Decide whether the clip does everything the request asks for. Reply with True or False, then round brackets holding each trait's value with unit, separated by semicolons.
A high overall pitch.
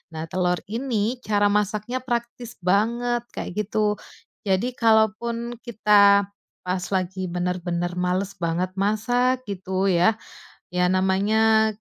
True (205 Hz)